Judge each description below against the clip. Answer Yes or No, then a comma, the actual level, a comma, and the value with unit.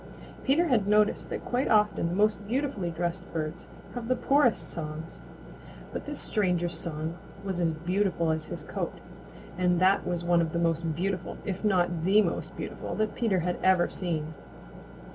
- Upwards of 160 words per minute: Yes, average, 170 wpm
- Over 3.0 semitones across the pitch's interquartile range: Yes, average, 3.9 semitones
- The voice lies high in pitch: No, medium, 180 Hz